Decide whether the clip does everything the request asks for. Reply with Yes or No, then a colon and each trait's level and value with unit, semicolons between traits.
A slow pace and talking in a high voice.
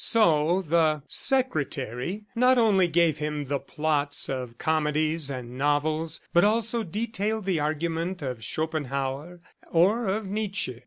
No: slow, 125 wpm; medium, 160 Hz